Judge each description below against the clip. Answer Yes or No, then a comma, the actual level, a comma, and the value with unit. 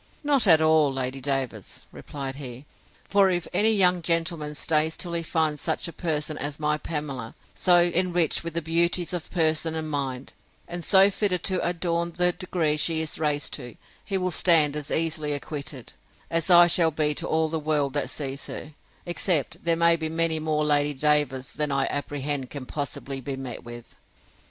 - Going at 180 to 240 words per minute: Yes, average, 190 wpm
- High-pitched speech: No, medium, 155 Hz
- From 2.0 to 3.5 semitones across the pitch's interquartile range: Yes, average, 2.9 semitones